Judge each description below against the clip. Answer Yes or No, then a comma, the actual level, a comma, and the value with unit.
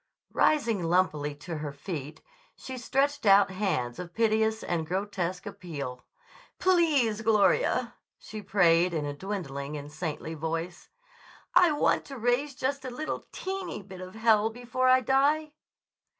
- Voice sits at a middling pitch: No, high, 200 Hz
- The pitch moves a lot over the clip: Yes, wide, 7.6 semitones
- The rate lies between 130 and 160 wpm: Yes, average, 140 wpm